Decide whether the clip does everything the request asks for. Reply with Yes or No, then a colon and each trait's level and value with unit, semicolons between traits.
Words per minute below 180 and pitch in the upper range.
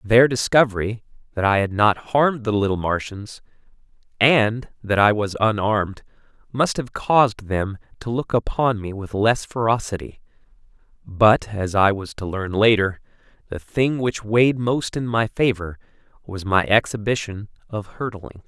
No: average, 150 wpm; low, 110 Hz